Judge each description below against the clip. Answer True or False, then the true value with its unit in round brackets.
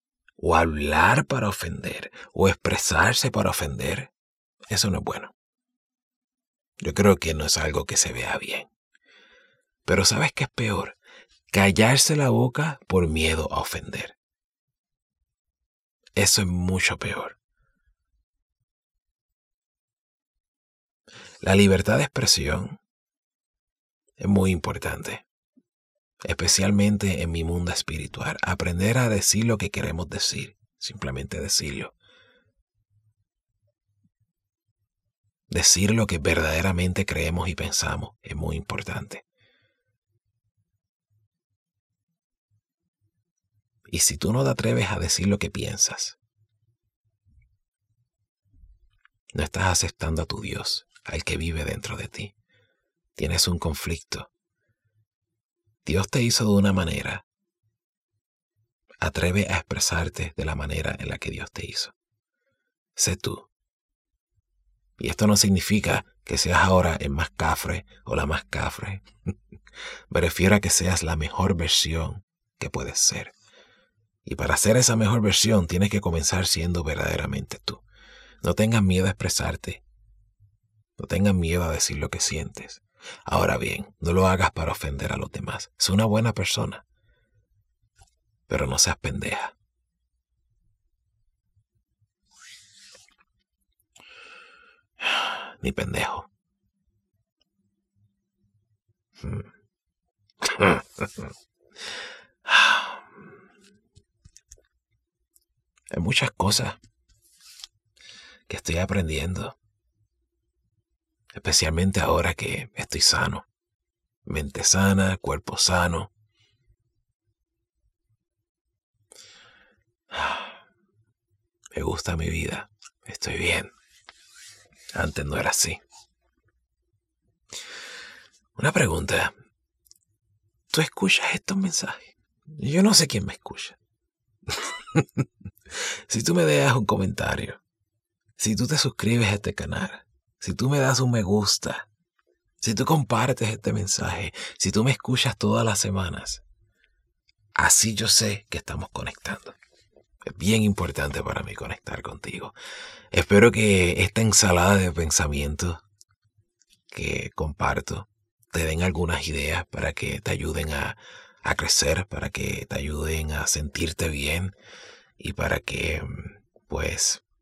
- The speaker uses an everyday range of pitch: True (4.0 semitones)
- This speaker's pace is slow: True (105 wpm)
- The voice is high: False (100 Hz)